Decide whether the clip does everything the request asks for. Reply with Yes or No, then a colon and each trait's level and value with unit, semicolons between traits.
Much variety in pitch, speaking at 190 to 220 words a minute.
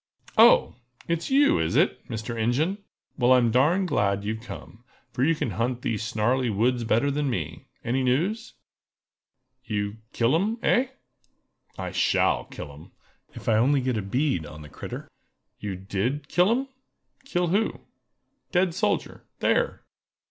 No: wide, 7.2 semitones; average, 145 wpm